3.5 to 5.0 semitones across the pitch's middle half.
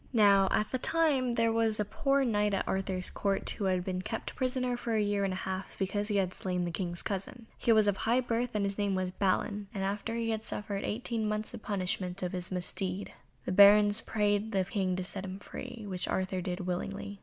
No: average, 2.8 semitones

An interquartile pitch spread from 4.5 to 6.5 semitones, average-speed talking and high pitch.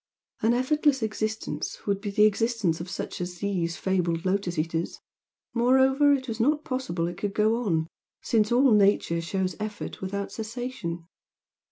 Yes: average, 5.2 semitones; average, 155 wpm; high, 210 Hz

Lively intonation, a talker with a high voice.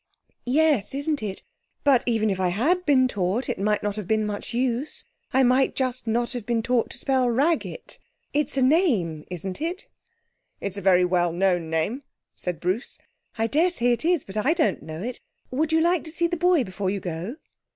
Yes: wide, 6.8 semitones; high, 240 Hz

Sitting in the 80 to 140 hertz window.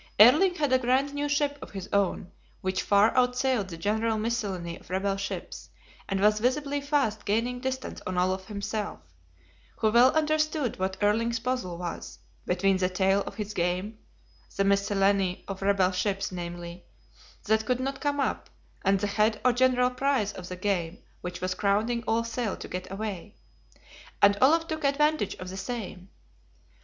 No: high, 210 Hz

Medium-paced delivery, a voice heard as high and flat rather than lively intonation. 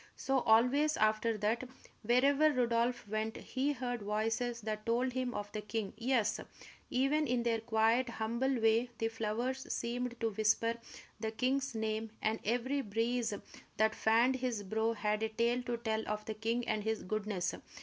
Yes: average, 165 wpm; high, 230 Hz; narrow, 2.3 semitones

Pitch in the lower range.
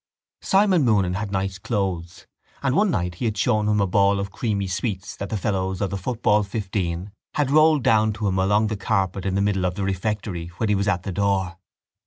Yes: low, 100 Hz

